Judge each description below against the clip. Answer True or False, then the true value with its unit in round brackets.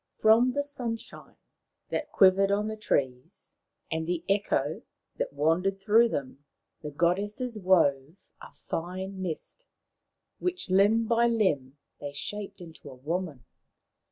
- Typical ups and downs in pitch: False (5.8 semitones)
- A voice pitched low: False (190 Hz)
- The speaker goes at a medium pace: False (130 wpm)